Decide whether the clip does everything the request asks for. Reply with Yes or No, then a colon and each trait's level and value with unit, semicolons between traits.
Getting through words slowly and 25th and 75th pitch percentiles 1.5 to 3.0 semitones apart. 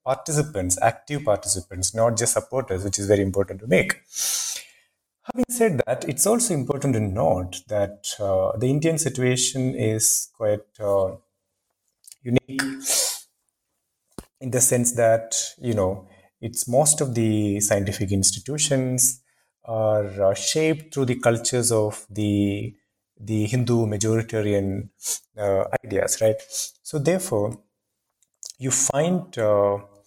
No: slow, 120 wpm; average, 4.7 semitones